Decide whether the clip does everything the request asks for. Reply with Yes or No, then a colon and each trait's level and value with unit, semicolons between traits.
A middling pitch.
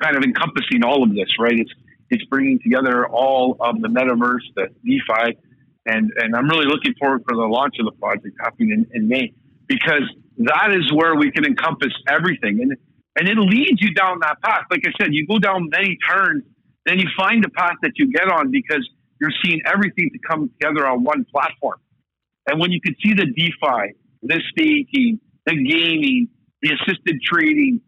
No: high, 195 Hz